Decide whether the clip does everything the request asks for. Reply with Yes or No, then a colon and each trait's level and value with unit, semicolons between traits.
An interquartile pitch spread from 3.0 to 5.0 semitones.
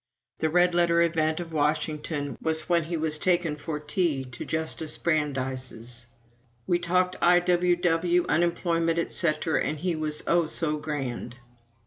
No: narrow, 2.4 semitones